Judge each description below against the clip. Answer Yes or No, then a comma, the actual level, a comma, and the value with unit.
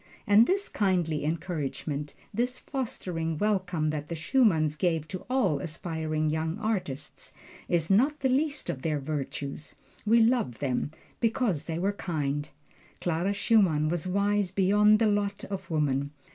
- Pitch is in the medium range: Yes, medium, 175 Hz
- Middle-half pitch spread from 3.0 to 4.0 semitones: No, average, 5.3 semitones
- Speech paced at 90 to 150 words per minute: Yes, average, 145 wpm